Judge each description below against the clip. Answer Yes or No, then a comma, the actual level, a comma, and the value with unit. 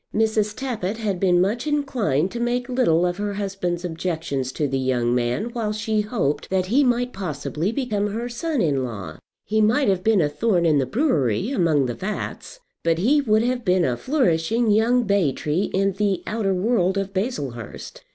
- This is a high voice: Yes, high, 195 Hz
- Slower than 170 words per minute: No, average, 190 wpm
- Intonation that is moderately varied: No, wide, 6.1 semitones